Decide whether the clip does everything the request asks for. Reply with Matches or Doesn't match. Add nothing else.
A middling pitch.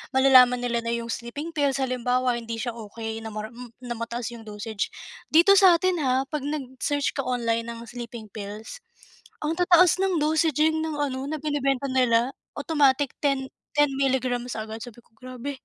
Doesn't match